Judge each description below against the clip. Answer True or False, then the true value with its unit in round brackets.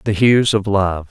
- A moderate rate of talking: False (220 wpm)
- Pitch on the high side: False (100 Hz)